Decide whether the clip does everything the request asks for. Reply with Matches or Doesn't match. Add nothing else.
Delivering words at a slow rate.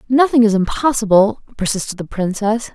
Matches